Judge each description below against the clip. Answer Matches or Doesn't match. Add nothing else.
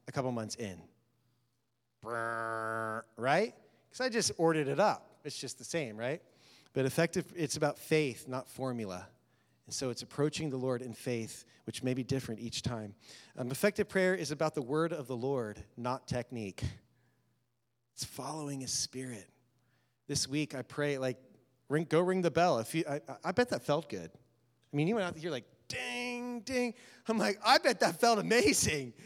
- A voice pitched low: Matches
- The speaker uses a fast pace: Doesn't match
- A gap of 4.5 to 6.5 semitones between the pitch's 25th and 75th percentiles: Matches